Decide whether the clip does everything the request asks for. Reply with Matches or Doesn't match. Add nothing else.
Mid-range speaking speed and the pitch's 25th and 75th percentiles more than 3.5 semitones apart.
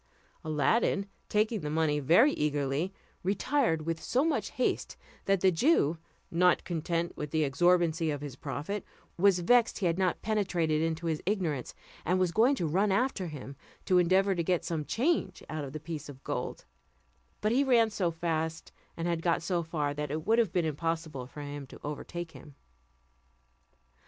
Matches